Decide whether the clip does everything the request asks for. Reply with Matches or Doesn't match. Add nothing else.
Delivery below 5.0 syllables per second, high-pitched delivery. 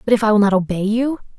Doesn't match